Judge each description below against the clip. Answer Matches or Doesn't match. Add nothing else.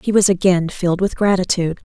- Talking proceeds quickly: Doesn't match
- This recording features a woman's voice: Matches